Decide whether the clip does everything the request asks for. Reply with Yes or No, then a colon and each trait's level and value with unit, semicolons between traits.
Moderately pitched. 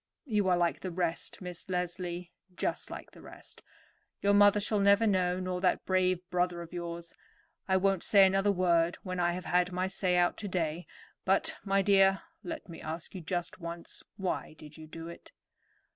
Yes: medium, 180 Hz